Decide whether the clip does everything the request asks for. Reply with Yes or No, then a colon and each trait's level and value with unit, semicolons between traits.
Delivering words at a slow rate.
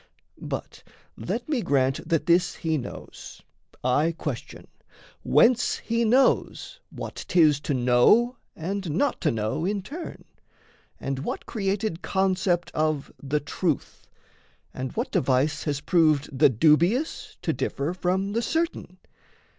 Yes: slow, 130 wpm